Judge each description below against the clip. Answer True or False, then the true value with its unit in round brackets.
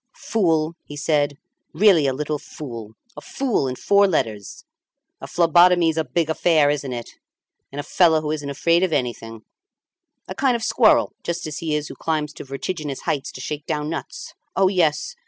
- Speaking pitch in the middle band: True (155 Hz)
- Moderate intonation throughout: True (3.4 semitones)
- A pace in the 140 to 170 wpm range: False (180 wpm)